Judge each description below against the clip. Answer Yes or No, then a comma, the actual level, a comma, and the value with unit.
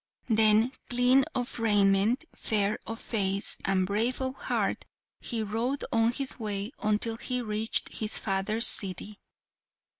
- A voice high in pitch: Yes, high, 220 Hz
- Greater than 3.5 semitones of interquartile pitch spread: No, average, 2.8 semitones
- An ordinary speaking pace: No, slow, 130 wpm